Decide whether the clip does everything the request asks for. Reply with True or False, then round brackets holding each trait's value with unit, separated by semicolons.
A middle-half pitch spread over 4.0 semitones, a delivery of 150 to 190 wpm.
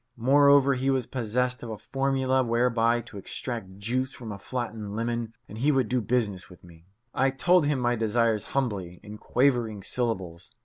False (3.6 semitones; 175 wpm)